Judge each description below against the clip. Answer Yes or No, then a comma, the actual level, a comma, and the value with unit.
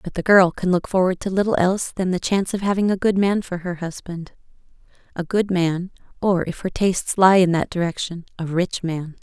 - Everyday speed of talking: No, fast, 215 wpm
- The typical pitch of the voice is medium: Yes, medium, 180 Hz